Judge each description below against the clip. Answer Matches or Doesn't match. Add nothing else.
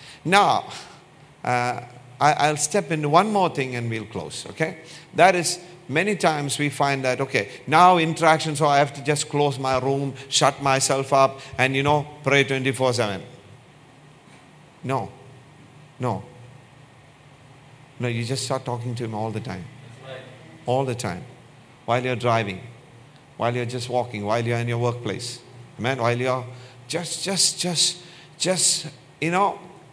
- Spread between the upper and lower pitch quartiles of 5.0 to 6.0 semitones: Doesn't match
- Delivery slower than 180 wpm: Matches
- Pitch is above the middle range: Doesn't match